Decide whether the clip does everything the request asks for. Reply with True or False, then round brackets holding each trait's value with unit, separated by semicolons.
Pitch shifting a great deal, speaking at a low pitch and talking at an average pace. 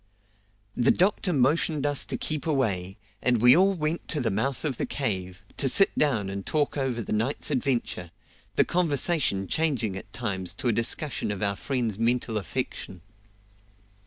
True (6.2 semitones; 125 Hz; 165 wpm)